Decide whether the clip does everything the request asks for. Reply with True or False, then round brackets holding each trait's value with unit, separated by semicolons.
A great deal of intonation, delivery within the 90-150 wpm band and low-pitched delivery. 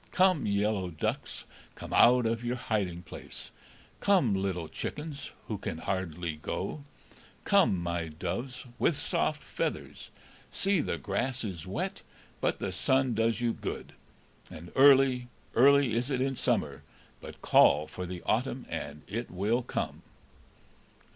True (6.6 semitones; 140 wpm; 115 Hz)